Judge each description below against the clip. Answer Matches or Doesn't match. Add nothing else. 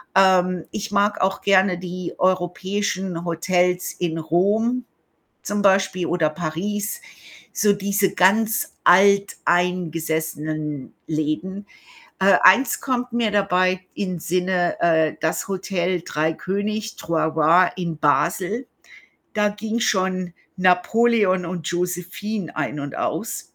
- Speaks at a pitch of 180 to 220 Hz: Matches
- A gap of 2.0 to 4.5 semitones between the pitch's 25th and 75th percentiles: Matches